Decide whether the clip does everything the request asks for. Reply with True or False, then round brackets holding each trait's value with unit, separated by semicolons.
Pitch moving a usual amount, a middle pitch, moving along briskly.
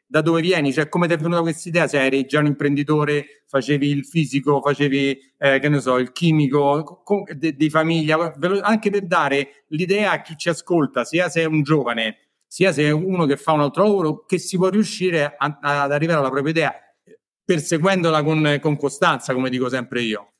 True (3.3 semitones; 150 Hz; 205 wpm)